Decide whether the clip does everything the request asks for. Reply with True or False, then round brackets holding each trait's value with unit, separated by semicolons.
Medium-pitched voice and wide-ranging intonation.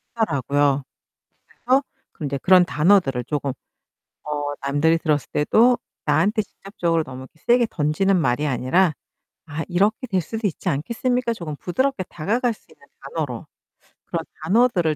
True (170 Hz; 6.8 semitones)